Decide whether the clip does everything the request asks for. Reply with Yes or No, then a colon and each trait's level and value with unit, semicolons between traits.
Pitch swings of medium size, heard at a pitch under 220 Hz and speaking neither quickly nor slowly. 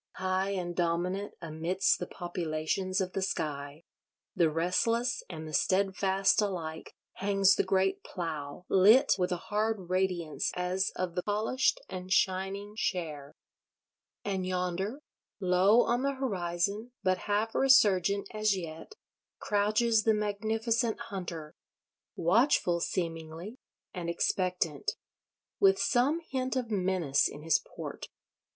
No: average, 3.5 semitones; high, 190 Hz; slow, 120 wpm